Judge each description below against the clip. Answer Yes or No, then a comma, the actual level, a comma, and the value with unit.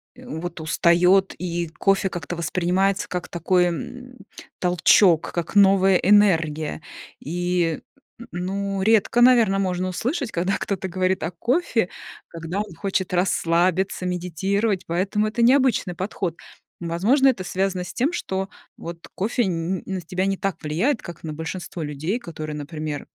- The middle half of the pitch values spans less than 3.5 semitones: Yes, average, 2.7 semitones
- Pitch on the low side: No, medium, 185 Hz